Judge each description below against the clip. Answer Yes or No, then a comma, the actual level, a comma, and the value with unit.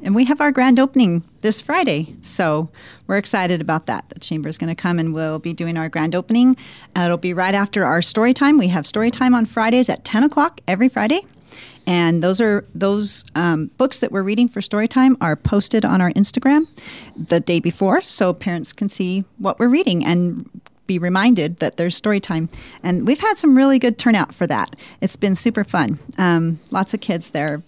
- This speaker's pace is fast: Yes, fast, 210 wpm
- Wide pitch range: Yes, wide, 6.1 semitones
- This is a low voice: No, high, 195 Hz